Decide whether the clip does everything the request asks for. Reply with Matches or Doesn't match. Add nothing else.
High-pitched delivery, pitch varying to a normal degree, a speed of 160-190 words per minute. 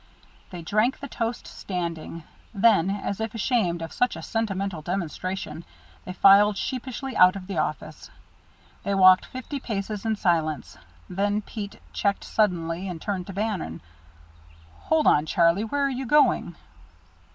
Doesn't match